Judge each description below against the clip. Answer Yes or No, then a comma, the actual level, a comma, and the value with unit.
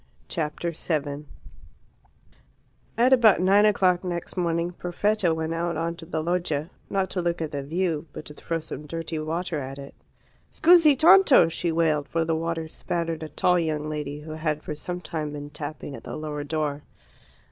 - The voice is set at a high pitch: No, medium, 165 Hz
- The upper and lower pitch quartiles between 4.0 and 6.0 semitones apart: No, narrow, 2.6 semitones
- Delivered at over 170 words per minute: Yes, average, 180 wpm